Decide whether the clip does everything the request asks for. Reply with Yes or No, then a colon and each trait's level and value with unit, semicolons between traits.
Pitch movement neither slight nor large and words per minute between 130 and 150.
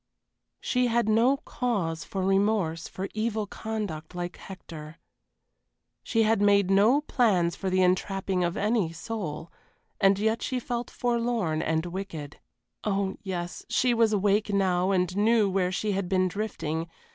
Yes: average, 3.7 semitones; average, 145 wpm